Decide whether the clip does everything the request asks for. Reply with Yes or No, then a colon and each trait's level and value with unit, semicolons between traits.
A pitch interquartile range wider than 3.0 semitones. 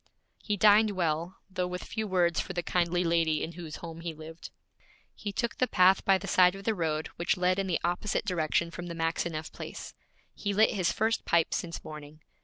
No: average, 2.7 semitones